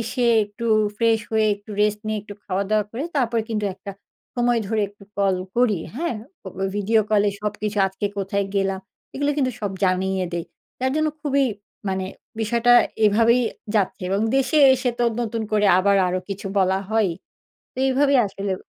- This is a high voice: Yes, high, 210 Hz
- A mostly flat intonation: No, average, 3.1 semitones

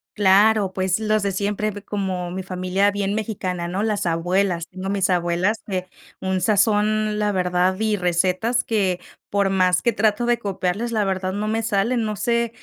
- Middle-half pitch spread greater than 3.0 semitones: No, narrow, 2.6 semitones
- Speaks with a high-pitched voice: Yes, high, 200 Hz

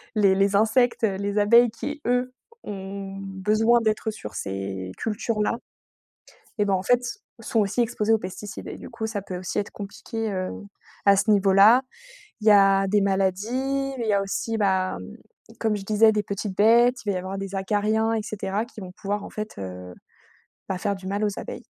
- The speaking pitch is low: No, high, 205 Hz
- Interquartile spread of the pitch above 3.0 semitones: No, narrow, 2.4 semitones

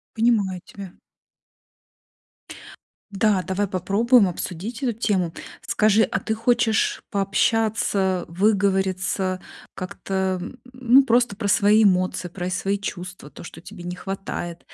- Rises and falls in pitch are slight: No, average, 3.0 semitones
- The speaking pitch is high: Yes, high, 195 Hz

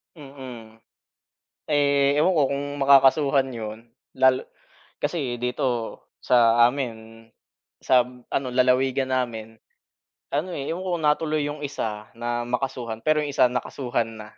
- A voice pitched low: Yes, low, 130 Hz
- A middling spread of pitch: Yes, average, 3.1 semitones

